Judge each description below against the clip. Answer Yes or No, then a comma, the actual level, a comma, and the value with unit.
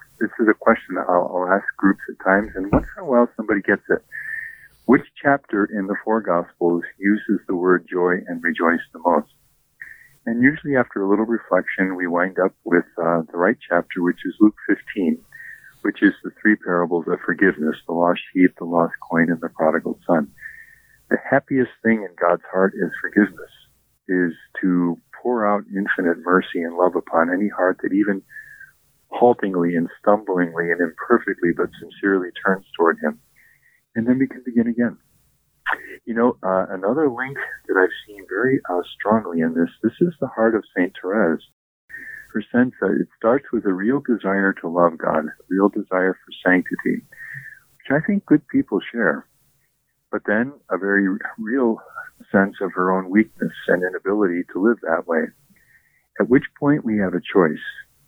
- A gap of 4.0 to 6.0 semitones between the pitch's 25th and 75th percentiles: Yes, wide, 5.4 semitones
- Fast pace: No, average, 175 wpm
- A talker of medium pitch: No, low, 100 Hz